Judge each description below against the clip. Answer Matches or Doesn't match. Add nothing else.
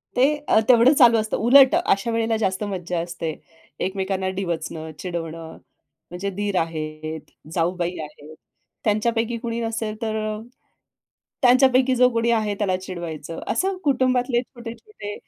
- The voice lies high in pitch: Matches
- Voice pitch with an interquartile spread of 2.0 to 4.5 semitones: Doesn't match